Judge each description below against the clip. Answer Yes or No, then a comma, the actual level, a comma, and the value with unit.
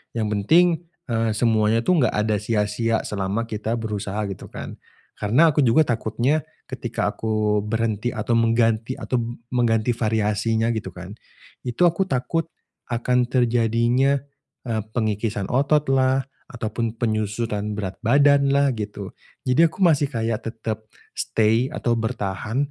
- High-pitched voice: No, low, 115 Hz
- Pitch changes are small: No, average, 3.2 semitones